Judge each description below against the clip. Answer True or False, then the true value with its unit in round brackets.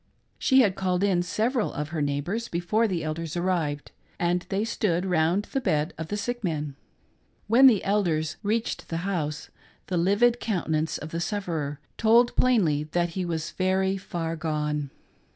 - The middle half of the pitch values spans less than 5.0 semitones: True (4.5 semitones)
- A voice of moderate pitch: True (175 Hz)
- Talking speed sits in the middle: True (165 wpm)